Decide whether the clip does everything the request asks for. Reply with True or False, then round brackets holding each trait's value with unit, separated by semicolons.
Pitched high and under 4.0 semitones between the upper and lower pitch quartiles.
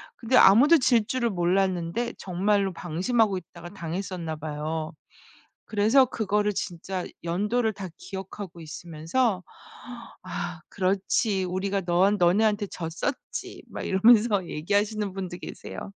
True (195 Hz; 3.4 semitones)